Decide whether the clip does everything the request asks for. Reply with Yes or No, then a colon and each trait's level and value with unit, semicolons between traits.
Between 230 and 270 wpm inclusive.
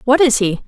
Yes: fast, 265 wpm